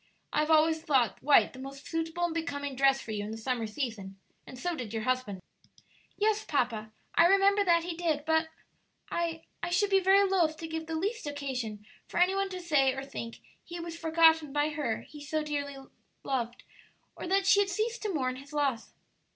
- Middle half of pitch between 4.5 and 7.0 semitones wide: Yes, average, 4.8 semitones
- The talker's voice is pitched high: Yes, very high, 310 Hz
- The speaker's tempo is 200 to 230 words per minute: Yes, fast, 205 wpm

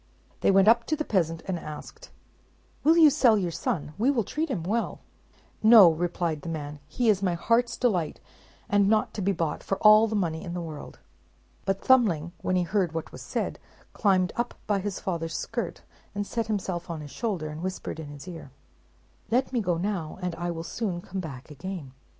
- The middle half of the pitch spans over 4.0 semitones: Yes, average, 4.9 semitones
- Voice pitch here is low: No, medium, 185 Hz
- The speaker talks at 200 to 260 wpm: Yes, fast, 205 wpm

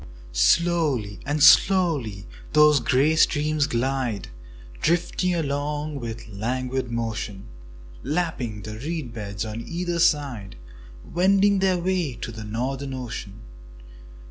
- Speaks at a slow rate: Yes, slow, 115 wpm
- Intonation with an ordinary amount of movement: No, wide, 6.2 semitones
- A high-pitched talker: No, low, 135 Hz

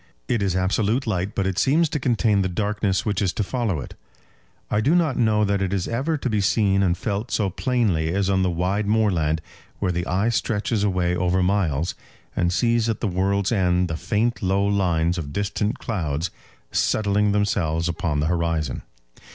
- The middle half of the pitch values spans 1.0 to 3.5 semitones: Yes, average, 3.2 semitones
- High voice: No, low, 100 Hz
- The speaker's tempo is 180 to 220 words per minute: Yes, average, 190 wpm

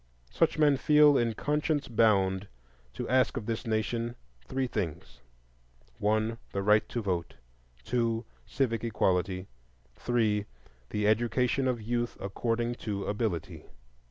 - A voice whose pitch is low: Yes, low, 115 Hz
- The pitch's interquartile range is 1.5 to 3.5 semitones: Yes, average, 2.7 semitones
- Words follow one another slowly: Yes, slow, 125 wpm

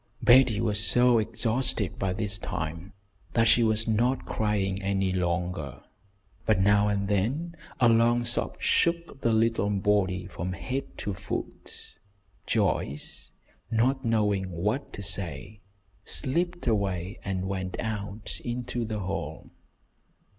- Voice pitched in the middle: No, low, 105 Hz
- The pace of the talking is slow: Yes, slow, 130 wpm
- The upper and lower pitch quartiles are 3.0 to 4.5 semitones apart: Yes, average, 3.6 semitones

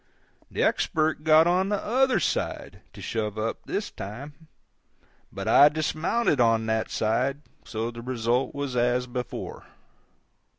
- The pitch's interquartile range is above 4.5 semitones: Yes, wide, 5.4 semitones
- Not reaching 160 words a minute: Yes, slow, 135 wpm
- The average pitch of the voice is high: No, low, 130 Hz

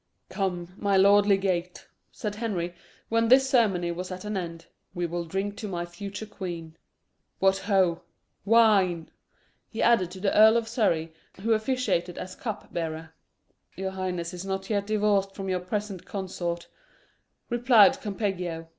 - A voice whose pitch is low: No, high, 195 Hz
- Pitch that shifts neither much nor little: Yes, average, 3.3 semitones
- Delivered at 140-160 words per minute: Yes, average, 150 wpm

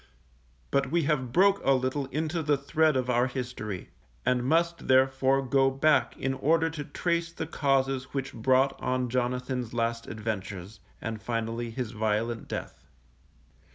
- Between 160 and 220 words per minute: No, average, 150 wpm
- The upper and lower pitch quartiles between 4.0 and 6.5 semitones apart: No, average, 3.3 semitones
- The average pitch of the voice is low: Yes, low, 130 Hz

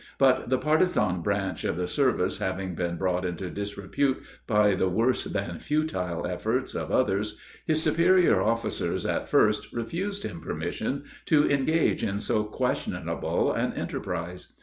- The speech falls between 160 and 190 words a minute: No, average, 145 wpm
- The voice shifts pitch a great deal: Yes, wide, 7.4 semitones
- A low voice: Yes, low, 105 Hz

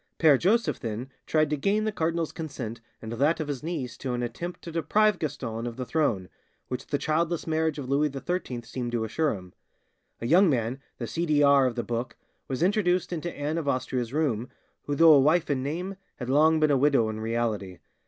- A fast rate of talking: Yes, fast, 210 wpm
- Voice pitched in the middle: Yes, medium, 145 Hz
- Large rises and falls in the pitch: No, average, 4.9 semitones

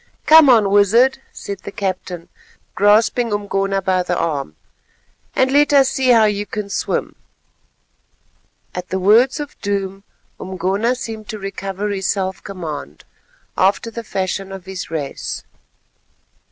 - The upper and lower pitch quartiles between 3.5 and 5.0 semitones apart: No, average, 3.1 semitones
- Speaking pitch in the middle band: No, high, 200 Hz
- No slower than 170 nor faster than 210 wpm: No, slow, 135 wpm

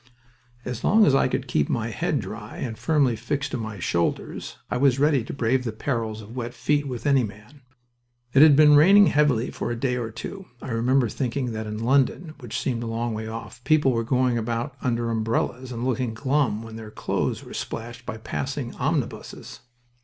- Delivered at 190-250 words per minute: Yes, average, 200 wpm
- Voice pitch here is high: No, low, 125 Hz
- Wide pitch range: No, average, 3.5 semitones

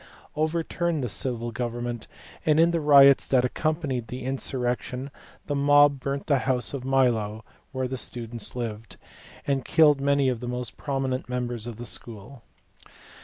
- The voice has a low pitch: Yes, low, 130 Hz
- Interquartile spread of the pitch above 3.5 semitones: No, average, 2.7 semitones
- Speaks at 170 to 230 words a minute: No, average, 155 wpm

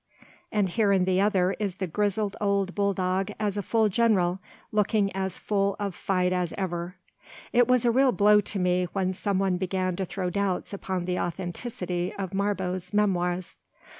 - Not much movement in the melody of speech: Yes, narrow, 2.1 semitones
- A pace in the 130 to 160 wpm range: No, average, 180 wpm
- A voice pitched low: No, high, 195 Hz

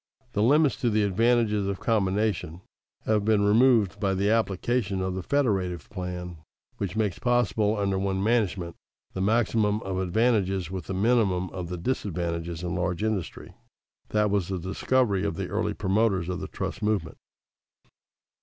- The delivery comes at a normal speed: Yes, average, 155 wpm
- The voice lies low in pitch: Yes, low, 100 Hz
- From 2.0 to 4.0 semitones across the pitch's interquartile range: Yes, average, 3.0 semitones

